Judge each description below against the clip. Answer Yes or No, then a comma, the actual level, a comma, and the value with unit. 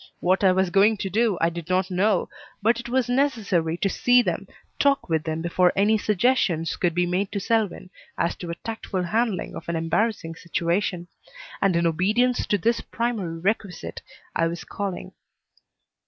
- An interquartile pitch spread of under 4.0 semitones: No, average, 4.4 semitones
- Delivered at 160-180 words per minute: Yes, average, 175 wpm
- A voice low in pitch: No, high, 190 Hz